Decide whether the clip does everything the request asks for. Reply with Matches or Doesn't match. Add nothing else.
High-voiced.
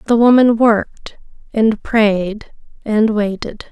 Matches